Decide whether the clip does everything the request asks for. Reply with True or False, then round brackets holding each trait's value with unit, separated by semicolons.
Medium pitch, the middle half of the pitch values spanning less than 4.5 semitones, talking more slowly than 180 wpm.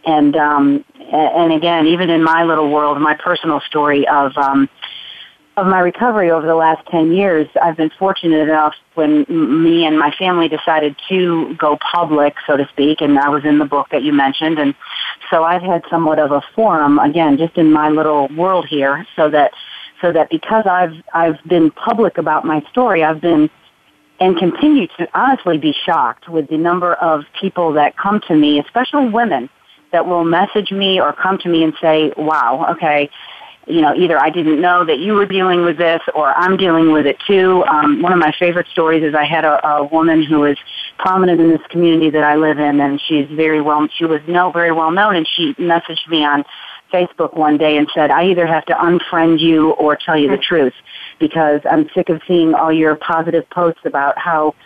False (165 Hz; 2.7 semitones; 205 wpm)